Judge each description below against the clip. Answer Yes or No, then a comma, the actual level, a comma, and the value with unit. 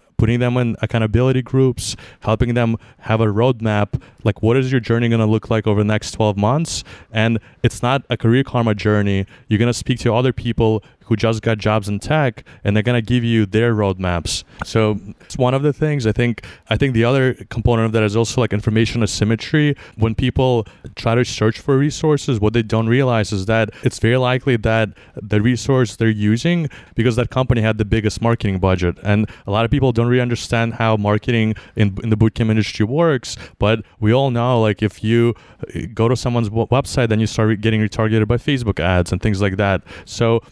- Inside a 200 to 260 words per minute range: Yes, fast, 205 wpm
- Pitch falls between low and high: No, low, 115 Hz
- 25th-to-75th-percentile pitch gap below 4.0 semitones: Yes, narrow, 2.5 semitones